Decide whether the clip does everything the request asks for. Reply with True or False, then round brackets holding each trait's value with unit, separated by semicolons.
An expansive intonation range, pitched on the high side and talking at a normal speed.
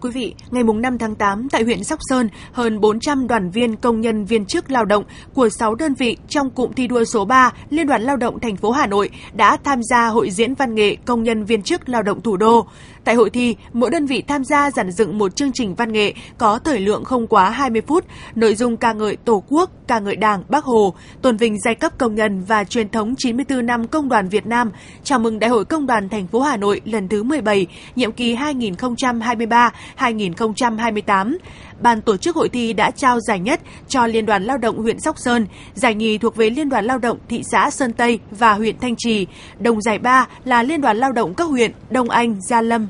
False (2.6 semitones; 235 Hz; 230 wpm)